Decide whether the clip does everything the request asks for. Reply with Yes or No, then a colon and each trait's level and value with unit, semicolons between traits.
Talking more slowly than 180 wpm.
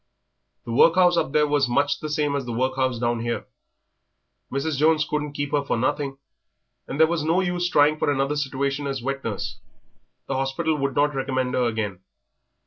No: average, 185 wpm